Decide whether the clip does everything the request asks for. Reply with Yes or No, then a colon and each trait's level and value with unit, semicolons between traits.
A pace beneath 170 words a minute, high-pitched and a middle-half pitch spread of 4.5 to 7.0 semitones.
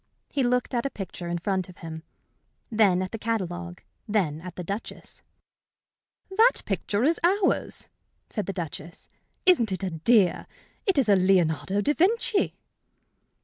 Yes: average, 145 wpm; high, 195 Hz; wide, 5.5 semitones